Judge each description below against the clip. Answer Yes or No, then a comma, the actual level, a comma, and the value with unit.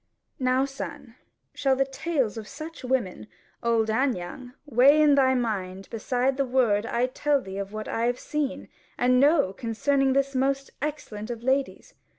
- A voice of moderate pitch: No, very high, 255 Hz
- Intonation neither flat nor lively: Yes, average, 3.4 semitones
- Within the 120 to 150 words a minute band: No, average, 165 wpm